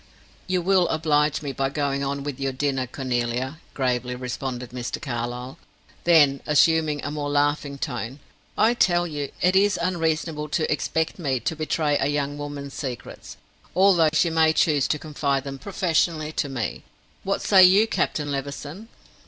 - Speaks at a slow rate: No, average, 160 wpm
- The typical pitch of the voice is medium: Yes, medium, 145 Hz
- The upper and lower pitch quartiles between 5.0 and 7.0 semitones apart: No, average, 3.0 semitones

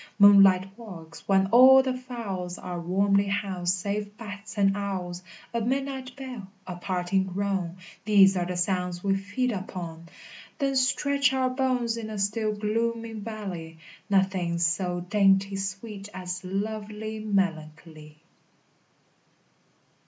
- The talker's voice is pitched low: No, high, 200 Hz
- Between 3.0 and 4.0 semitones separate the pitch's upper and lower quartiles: Yes, average, 3.3 semitones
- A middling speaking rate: No, slow, 125 wpm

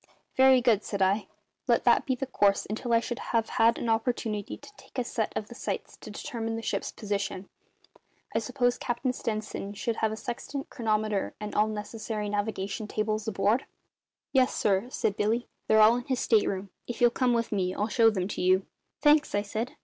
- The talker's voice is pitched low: No, high, 220 Hz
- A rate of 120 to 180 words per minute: No, average, 195 wpm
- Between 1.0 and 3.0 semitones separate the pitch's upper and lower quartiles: Yes, average, 2.7 semitones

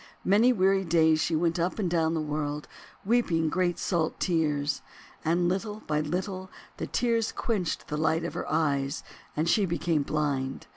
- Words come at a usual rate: Yes, average, 165 wpm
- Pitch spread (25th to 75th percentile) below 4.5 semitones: Yes, average, 3.4 semitones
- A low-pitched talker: No, medium, 165 Hz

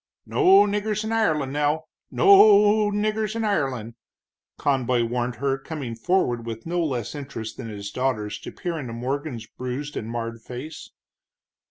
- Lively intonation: Yes, wide, 9.0 semitones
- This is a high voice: No, medium, 140 Hz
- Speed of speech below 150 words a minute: No, average, 160 wpm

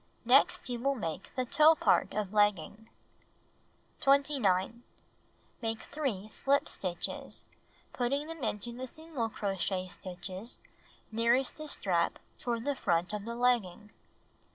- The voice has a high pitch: Yes, high, 230 Hz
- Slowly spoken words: Yes, slow, 125 wpm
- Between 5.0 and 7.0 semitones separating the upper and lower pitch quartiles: Yes, wide, 5.4 semitones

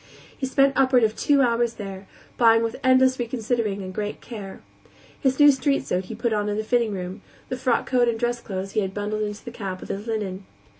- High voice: Yes, high, 225 Hz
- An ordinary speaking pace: No, fast, 220 wpm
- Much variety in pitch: No, average, 3.7 semitones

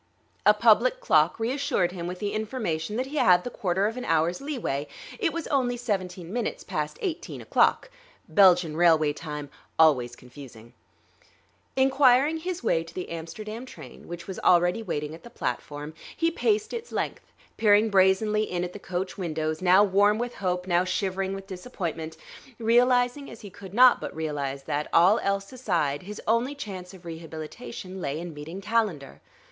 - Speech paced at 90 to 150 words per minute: No, average, 170 wpm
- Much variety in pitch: Yes, wide, 6.1 semitones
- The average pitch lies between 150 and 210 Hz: Yes, high, 190 Hz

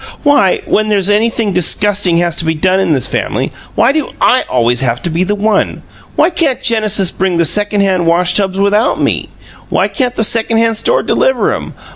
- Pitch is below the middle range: No, high, 200 Hz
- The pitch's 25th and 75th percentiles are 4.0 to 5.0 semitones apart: Yes, average, 4.3 semitones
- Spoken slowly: No, average, 200 wpm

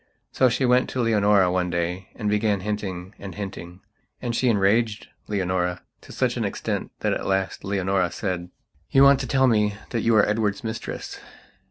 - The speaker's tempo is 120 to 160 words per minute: No, average, 180 wpm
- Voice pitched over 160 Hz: No, low, 105 Hz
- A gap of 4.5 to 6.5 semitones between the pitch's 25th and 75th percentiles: No, average, 3.5 semitones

